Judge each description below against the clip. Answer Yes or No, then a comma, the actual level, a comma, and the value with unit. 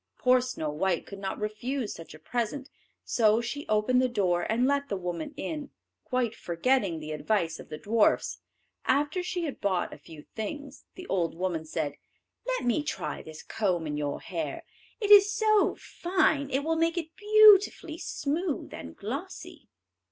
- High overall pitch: Yes, high, 240 Hz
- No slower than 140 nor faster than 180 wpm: Yes, average, 170 wpm